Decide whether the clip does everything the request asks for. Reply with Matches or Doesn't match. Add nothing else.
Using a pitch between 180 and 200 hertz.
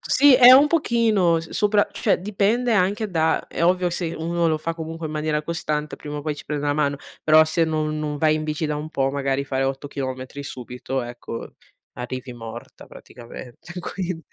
Doesn't match